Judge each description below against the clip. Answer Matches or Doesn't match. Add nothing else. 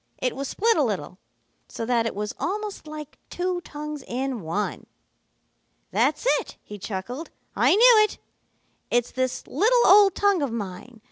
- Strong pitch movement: Matches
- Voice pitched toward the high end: Matches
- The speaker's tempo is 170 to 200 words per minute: Doesn't match